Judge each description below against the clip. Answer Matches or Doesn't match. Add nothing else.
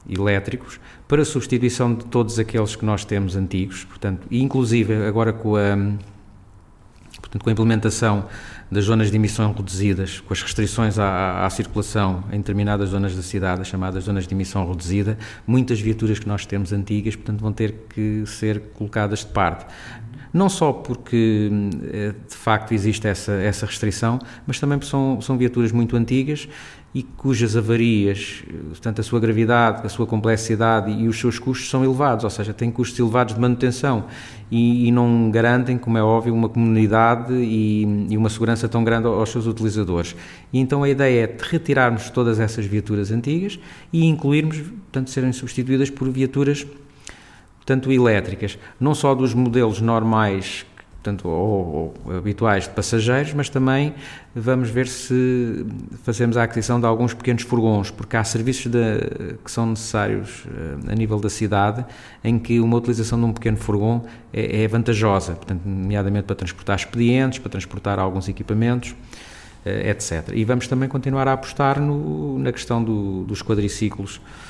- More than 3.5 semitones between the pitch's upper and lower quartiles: Doesn't match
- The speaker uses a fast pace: Doesn't match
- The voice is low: Matches